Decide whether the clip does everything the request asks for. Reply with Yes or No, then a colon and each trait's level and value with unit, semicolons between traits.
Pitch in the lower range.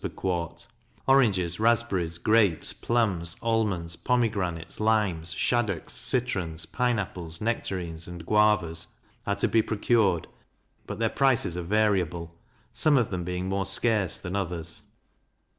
Yes: very low, 95 Hz